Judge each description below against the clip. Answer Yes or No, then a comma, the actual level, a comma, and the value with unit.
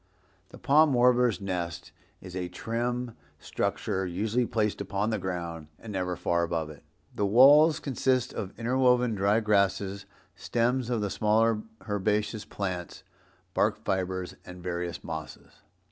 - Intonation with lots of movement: No, average, 4.6 semitones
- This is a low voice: Yes, low, 105 Hz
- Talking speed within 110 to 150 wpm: Yes, slow, 135 wpm